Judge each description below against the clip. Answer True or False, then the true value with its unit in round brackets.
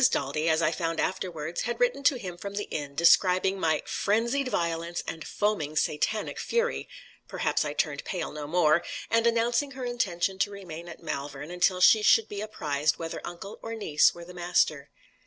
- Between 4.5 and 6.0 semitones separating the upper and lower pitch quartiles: True (5.2 semitones)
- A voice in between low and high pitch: True (175 Hz)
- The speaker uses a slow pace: False (180 wpm)